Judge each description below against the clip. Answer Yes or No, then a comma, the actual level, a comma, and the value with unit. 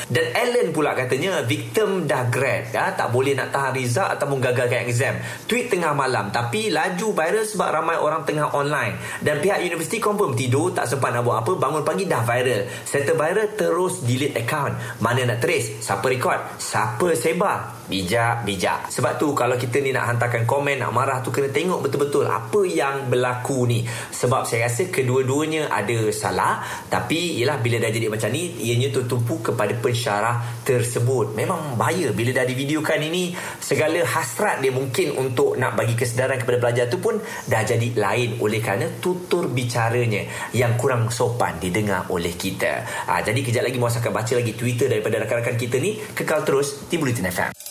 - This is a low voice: Yes, low, 125 Hz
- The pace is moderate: No, fast, 175 wpm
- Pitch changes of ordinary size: Yes, average, 3.1 semitones